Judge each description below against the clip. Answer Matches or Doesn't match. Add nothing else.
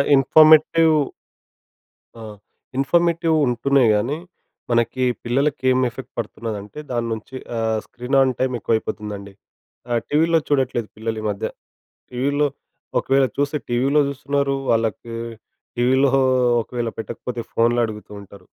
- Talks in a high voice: Doesn't match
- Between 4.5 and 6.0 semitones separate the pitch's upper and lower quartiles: Doesn't match